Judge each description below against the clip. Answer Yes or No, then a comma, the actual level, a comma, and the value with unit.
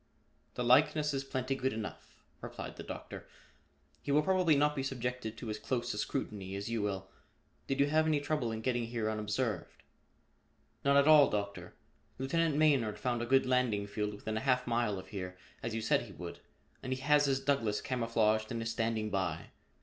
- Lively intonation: No, average, 4.3 semitones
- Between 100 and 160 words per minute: No, average, 195 wpm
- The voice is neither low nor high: No, low, 120 Hz